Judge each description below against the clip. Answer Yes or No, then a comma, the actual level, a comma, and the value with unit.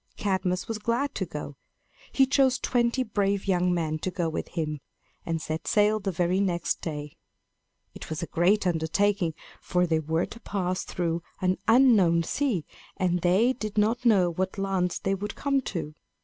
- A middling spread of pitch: Yes, average, 4.0 semitones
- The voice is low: No, medium, 185 Hz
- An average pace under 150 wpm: No, average, 175 wpm